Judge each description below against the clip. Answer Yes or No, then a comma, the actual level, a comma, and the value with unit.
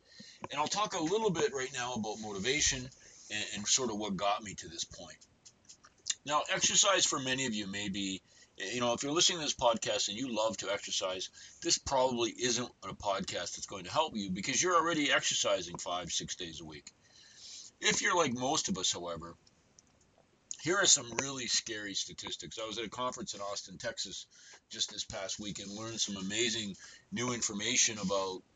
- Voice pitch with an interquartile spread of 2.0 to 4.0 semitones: No, average, 5.3 semitones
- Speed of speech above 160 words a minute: Yes, average, 195 wpm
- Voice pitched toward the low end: Yes, low, 120 Hz